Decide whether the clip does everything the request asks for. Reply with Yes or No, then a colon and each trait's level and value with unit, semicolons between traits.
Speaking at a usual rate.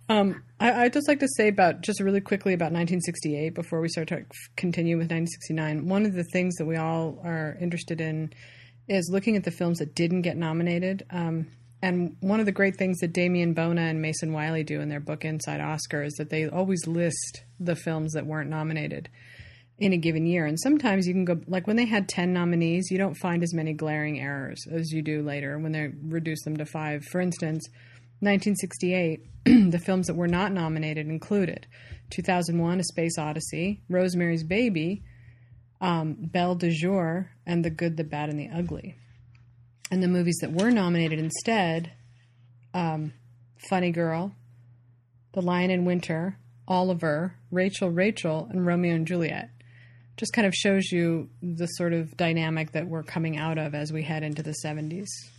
Yes: average, 180 wpm